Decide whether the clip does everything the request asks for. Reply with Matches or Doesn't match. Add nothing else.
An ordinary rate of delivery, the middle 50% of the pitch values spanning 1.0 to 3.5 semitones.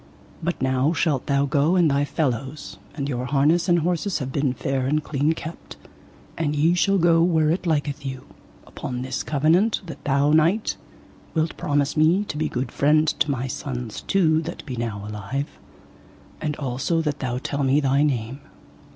Matches